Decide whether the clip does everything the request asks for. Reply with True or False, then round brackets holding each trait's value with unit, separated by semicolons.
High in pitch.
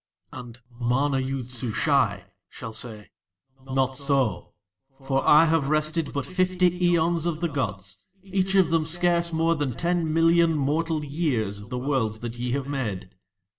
False (140 Hz)